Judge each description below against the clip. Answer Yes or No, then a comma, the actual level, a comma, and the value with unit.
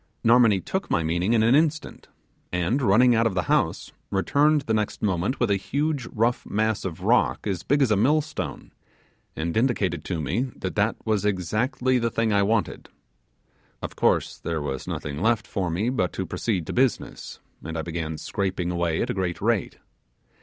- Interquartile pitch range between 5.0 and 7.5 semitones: Yes, wide, 5.5 semitones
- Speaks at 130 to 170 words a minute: No, average, 185 wpm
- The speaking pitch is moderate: No, low, 105 Hz